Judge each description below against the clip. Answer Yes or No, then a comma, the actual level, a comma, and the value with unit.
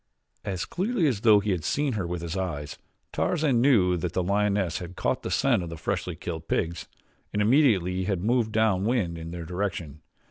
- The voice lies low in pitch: Yes, very low, 95 Hz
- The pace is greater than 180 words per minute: Yes, average, 200 wpm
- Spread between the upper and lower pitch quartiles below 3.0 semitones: No, average, 4.5 semitones